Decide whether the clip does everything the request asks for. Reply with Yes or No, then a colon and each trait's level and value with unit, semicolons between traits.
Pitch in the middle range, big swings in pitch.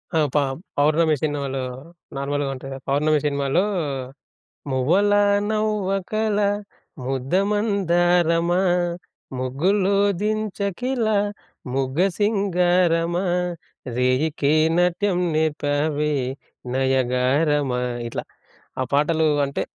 Yes: medium, 160 Hz; wide, 5.8 semitones